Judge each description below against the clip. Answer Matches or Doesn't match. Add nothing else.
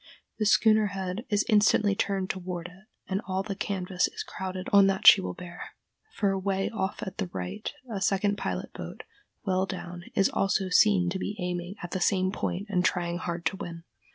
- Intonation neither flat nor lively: Doesn't match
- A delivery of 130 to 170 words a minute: Doesn't match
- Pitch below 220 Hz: Matches